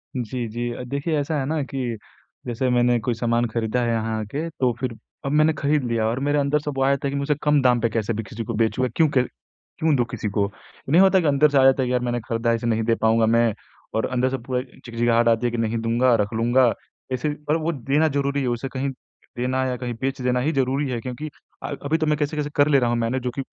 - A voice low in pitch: Yes, low, 125 Hz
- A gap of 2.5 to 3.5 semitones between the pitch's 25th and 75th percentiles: Yes, average, 3.2 semitones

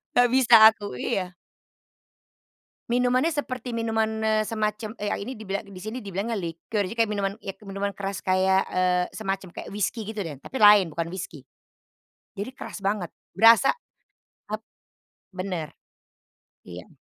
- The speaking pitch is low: No, high, 205 Hz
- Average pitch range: Yes, average, 3.0 semitones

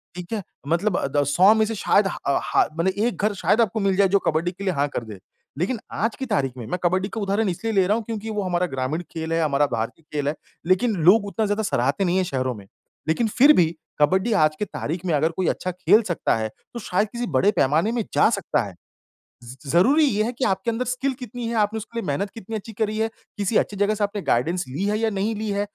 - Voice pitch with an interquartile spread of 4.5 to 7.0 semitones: Yes, average, 5.0 semitones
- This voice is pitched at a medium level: No, high, 195 Hz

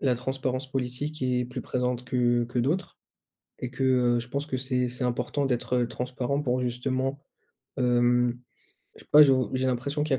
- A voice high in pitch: No, low, 125 Hz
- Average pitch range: No, narrow, 1.5 semitones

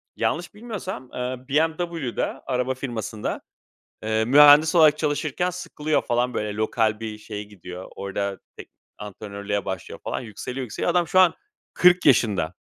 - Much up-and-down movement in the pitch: Yes, wide, 6.7 semitones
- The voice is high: No, low, 125 Hz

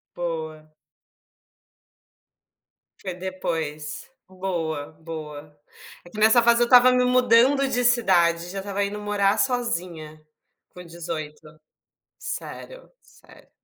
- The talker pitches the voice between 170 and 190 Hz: Yes, medium, 185 Hz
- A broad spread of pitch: Yes, wide, 6.6 semitones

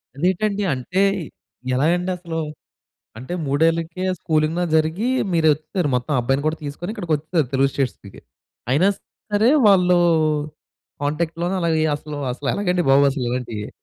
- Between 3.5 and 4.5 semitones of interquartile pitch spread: Yes, average, 3.9 semitones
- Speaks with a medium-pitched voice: Yes, medium, 160 Hz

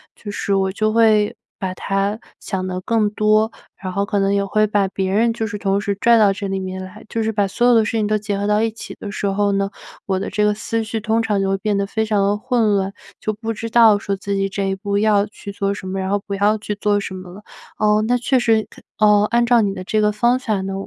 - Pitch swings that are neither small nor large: No, narrow, 1.8 semitones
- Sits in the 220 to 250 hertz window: No, high, 205 Hz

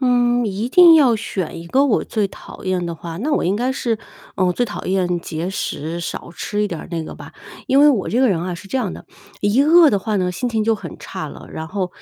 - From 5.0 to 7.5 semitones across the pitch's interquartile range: Yes, wide, 5.5 semitones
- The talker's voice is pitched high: Yes, high, 205 Hz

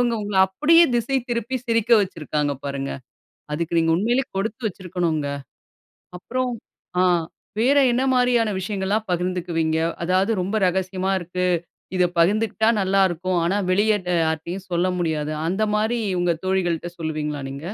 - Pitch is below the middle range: No, medium, 185 Hz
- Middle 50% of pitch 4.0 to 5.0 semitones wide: Yes, average, 4.3 semitones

